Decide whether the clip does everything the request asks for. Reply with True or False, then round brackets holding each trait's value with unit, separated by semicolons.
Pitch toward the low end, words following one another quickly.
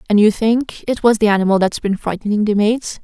False (215 Hz; 235 wpm)